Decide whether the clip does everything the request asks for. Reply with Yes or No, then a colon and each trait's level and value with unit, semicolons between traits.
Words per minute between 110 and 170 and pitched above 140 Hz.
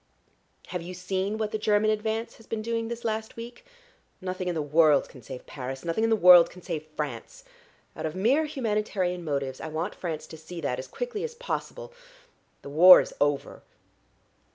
No: average, 190 wpm; medium, 185 Hz